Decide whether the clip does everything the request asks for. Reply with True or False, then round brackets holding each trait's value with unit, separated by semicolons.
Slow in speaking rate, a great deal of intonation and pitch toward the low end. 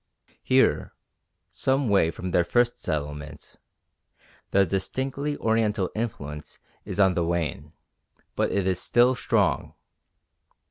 True (110 wpm; 6.2 semitones; 95 Hz)